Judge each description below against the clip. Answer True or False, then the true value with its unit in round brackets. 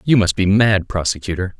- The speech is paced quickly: False (190 wpm)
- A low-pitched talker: True (100 Hz)